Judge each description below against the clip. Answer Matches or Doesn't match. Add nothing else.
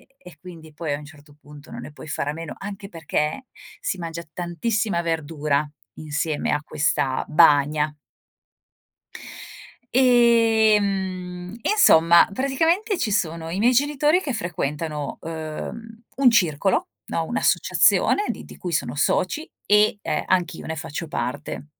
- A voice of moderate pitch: Matches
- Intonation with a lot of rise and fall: Matches